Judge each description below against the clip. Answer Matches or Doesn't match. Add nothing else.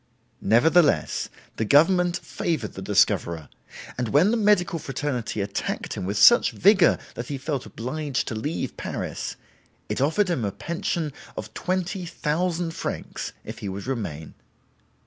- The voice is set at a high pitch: Doesn't match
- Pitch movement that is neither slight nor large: Doesn't match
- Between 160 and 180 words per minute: Doesn't match